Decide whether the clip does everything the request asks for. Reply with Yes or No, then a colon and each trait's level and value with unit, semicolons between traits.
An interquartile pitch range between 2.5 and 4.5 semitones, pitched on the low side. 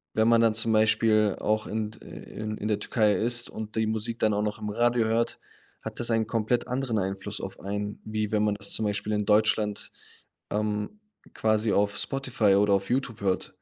No: narrow, 1.6 semitones; low, 110 Hz